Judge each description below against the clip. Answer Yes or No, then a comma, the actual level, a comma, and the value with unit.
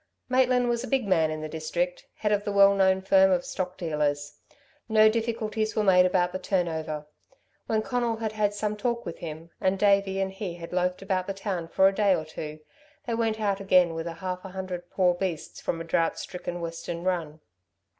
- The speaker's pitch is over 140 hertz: Yes, high, 190 Hz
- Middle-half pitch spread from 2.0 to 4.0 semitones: Yes, average, 3.6 semitones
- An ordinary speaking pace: No, fast, 210 wpm